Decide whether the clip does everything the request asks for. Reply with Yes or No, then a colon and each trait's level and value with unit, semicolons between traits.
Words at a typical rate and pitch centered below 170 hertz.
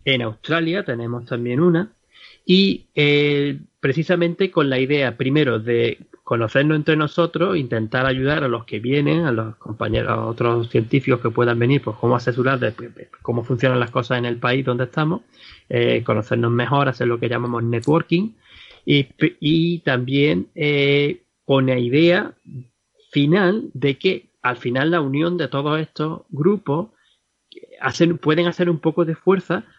Yes: average, 160 wpm; medium, 140 Hz